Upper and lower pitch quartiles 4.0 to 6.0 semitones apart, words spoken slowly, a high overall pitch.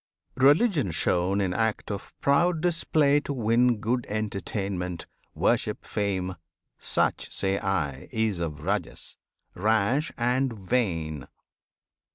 No: wide, 5.5 semitones; slow, 110 wpm; low, 105 Hz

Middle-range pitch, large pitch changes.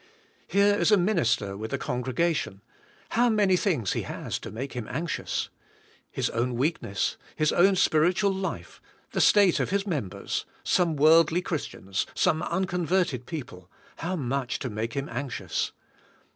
Yes: medium, 155 Hz; wide, 7.1 semitones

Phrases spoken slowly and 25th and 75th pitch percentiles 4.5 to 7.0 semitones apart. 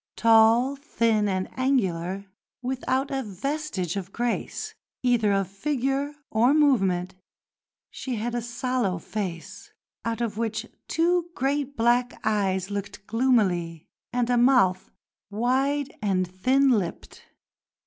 Yes: slow, 120 wpm; average, 5.1 semitones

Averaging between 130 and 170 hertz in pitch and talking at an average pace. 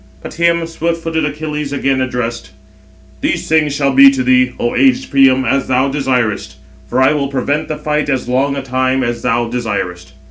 Yes: low, 135 Hz; average, 185 wpm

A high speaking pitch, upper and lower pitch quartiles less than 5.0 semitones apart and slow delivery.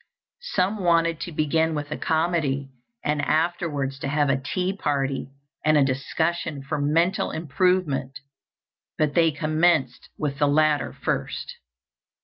No: medium, 155 Hz; average, 3.0 semitones; slow, 130 wpm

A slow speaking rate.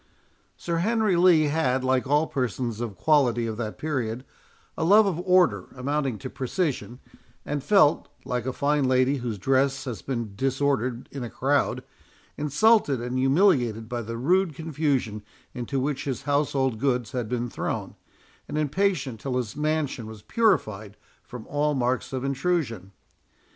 No: average, 155 wpm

